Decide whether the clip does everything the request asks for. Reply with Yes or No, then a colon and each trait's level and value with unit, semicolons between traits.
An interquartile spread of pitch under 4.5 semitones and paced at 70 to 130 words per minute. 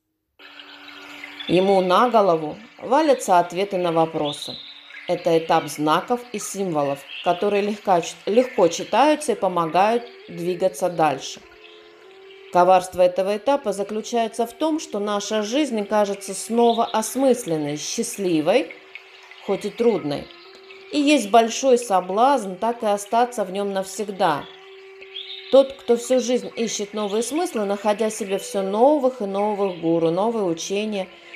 No: average, 4.9 semitones; average, 115 wpm